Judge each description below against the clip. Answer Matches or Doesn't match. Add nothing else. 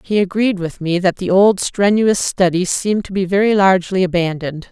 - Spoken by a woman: Matches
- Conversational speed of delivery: Matches